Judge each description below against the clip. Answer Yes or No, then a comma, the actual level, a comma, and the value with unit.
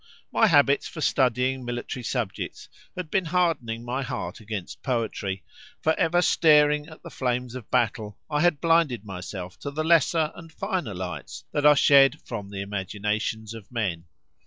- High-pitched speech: No, low, 125 Hz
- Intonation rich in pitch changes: Yes, wide, 6.1 semitones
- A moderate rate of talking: Yes, average, 160 wpm